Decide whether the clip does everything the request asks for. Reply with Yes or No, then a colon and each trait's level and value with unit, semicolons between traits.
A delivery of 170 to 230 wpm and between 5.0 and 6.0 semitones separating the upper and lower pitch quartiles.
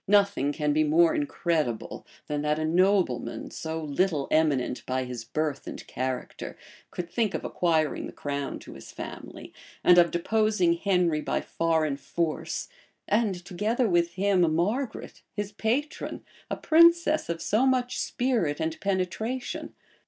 No: average, 145 wpm; average, 5.3 semitones